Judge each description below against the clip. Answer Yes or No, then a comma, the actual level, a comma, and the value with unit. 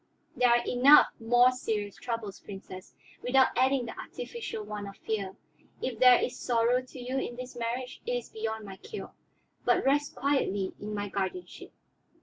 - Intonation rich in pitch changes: No, average, 3.5 semitones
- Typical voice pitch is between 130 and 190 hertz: No, high, 240 Hz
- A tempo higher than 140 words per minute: Yes, average, 165 wpm